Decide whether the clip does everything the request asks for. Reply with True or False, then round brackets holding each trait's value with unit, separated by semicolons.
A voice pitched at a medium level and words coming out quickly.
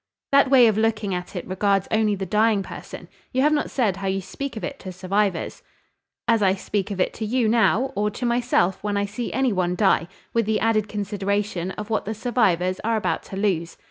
False (210 Hz; 220 wpm)